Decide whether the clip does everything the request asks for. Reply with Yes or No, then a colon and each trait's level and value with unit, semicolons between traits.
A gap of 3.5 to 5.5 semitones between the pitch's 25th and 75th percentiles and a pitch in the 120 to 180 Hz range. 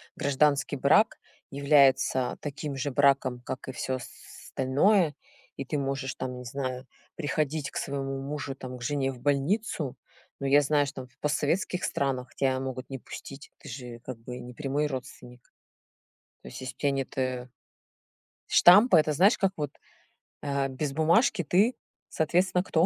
No: narrow, 2.4 semitones; medium, 140 Hz